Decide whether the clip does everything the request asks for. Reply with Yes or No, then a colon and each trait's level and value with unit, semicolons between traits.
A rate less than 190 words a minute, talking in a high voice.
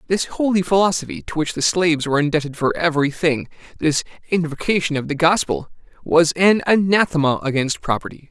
No: average, 160 wpm; medium, 165 Hz